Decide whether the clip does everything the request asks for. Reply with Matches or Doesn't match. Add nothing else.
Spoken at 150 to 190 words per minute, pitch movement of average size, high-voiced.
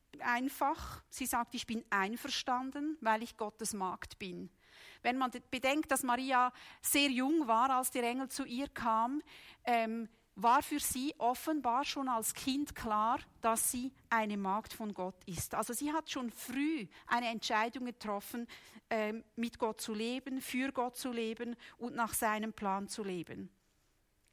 Matches